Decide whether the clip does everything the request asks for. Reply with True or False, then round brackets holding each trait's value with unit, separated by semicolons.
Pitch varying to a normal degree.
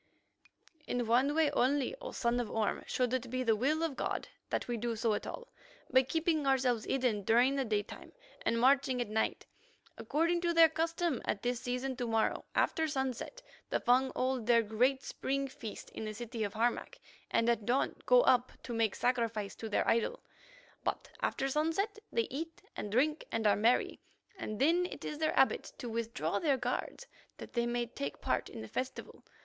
True (3.6 semitones)